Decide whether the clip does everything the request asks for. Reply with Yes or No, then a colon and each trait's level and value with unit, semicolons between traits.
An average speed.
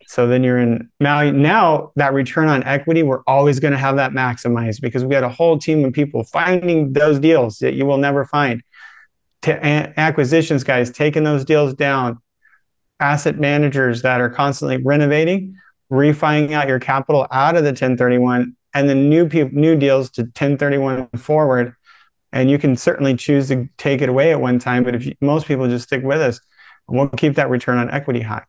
Yes: average, 195 wpm